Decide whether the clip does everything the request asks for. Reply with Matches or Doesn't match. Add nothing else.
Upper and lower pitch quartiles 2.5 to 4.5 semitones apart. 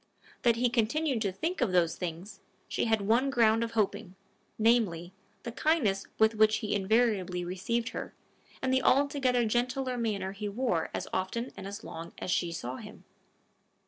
Matches